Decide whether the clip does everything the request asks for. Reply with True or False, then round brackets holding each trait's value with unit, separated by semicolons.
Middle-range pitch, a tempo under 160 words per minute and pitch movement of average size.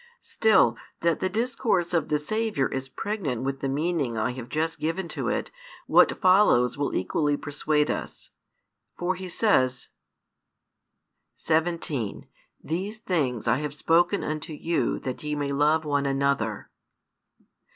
True (150 Hz; 140 wpm; 4.4 semitones)